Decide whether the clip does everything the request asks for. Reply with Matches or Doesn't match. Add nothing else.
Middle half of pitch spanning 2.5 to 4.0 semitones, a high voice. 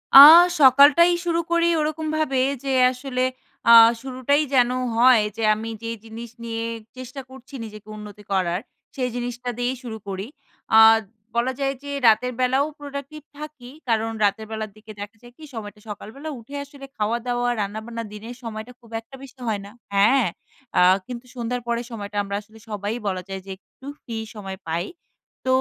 Matches